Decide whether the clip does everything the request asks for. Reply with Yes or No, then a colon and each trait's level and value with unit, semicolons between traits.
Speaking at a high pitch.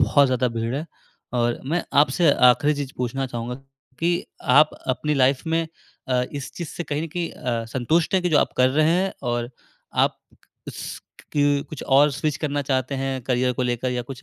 No: low, 135 Hz